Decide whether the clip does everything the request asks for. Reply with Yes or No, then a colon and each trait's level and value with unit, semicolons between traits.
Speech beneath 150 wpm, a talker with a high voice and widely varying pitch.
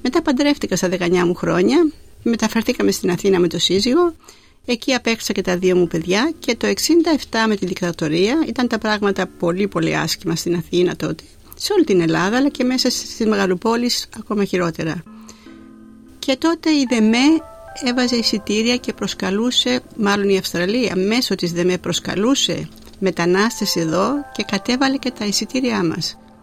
No: average, 155 wpm; high, 215 Hz; wide, 5.7 semitones